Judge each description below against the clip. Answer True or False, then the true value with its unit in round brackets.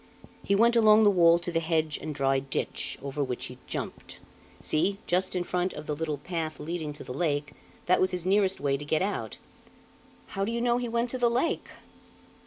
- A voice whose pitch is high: False (175 Hz)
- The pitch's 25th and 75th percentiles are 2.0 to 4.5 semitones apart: False (5.1 semitones)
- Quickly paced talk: True (210 wpm)